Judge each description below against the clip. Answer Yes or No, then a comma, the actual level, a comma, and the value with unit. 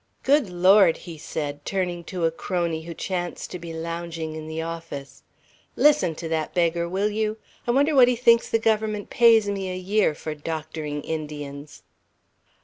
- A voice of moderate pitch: Yes, medium, 170 Hz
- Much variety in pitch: No, average, 4.7 semitones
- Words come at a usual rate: Yes, average, 170 wpm